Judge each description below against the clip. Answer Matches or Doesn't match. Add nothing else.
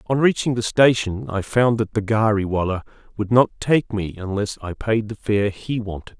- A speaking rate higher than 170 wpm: Matches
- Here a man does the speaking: Matches